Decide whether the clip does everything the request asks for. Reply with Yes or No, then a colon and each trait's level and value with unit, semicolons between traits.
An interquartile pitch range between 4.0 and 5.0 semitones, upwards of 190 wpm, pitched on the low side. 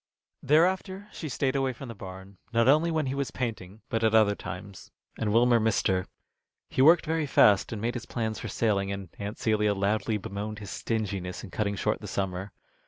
Yes: average, 4.6 semitones; average, 200 wpm; low, 110 Hz